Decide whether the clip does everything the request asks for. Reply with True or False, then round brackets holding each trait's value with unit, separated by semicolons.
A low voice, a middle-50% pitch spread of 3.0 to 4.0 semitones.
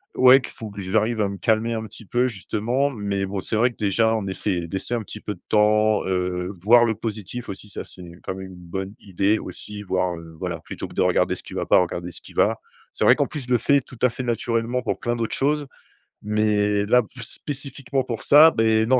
True (110 Hz; 3.6 semitones)